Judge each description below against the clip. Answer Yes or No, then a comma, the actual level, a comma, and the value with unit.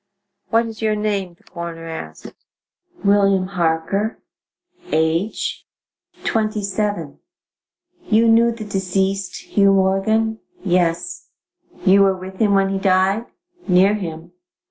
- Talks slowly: Yes, slow, 115 wpm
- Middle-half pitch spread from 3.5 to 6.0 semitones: No, average, 2.7 semitones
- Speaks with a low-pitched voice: No, high, 195 Hz